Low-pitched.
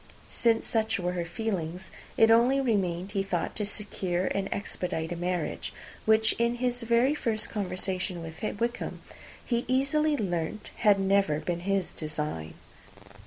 No: high, 200 Hz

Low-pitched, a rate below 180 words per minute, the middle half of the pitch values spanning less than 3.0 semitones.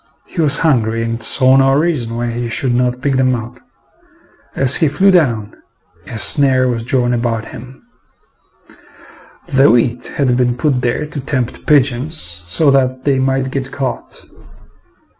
Yes: low, 130 Hz; average, 155 wpm; narrow, 2.5 semitones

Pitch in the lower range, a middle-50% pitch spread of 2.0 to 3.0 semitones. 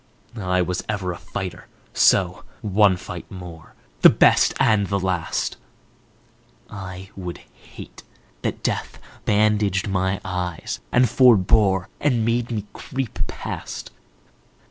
Yes: very low, 95 Hz; average, 2.7 semitones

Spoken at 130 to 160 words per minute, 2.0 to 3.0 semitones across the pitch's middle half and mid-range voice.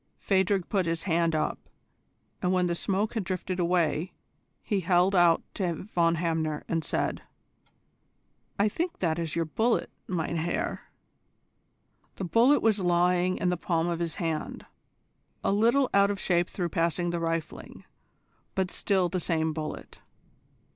Yes: average, 155 wpm; narrow, 2.5 semitones; medium, 175 Hz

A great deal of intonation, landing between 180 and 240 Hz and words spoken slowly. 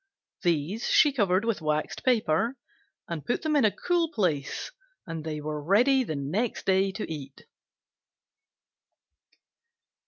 Yes: wide, 7.2 semitones; high, 190 Hz; slow, 125 wpm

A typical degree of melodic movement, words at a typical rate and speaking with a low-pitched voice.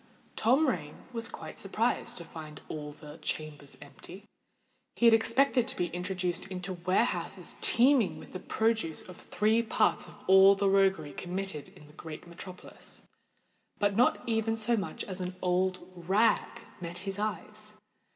No: average, 4.1 semitones; average, 155 wpm; high, 190 Hz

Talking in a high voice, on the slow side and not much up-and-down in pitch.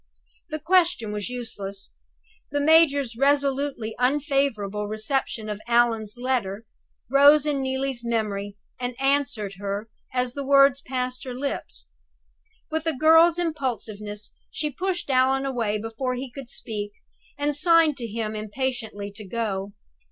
No: very high, 250 Hz; slow, 130 wpm; average, 4.6 semitones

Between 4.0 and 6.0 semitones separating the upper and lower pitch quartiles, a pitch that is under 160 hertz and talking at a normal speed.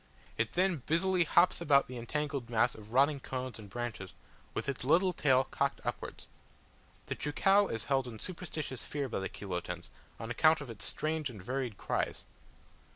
Yes: average, 5.1 semitones; low, 135 Hz; average, 170 wpm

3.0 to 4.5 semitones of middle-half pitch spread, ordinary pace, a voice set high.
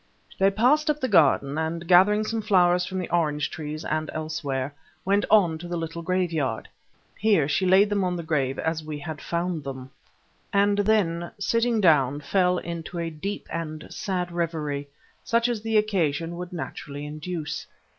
No: average, 4.2 semitones; average, 170 wpm; medium, 170 Hz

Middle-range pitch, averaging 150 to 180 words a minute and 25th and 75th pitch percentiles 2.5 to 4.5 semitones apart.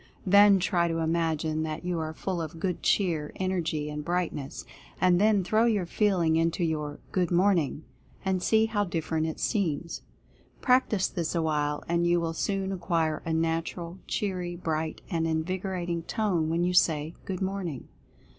Yes: medium, 170 Hz; average, 160 wpm; average, 2.8 semitones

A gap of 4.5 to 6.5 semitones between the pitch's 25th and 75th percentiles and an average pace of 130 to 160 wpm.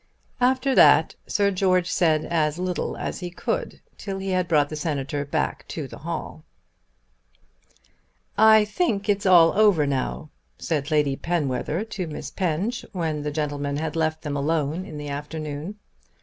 No: average, 4.1 semitones; average, 155 wpm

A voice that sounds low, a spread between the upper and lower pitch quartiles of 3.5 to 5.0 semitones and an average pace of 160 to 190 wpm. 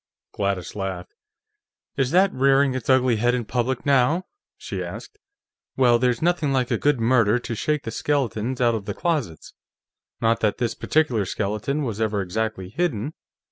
Yes: low, 120 Hz; average, 4.2 semitones; average, 165 wpm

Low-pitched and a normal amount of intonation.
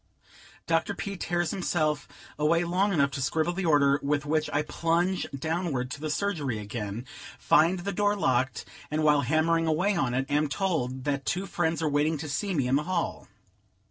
No: medium, 155 Hz; average, 3.7 semitones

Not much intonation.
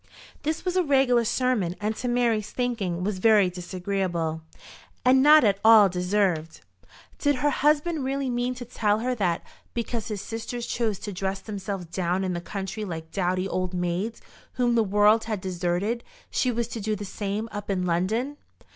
No: average, 4.6 semitones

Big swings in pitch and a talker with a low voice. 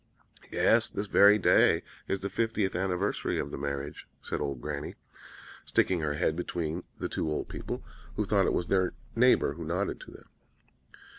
No: average, 4.4 semitones; very low, 90 Hz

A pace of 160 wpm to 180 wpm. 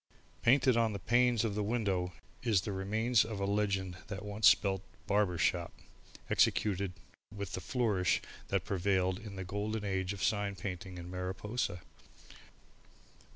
No: average, 150 wpm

